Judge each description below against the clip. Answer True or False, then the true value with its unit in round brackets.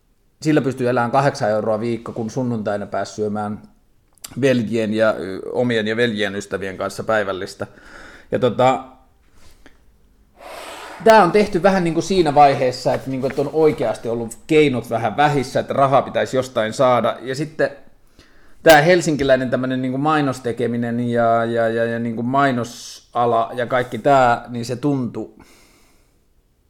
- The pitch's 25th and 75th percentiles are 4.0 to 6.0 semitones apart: False (3.4 semitones)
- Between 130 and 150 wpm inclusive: True (140 wpm)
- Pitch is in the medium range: False (125 Hz)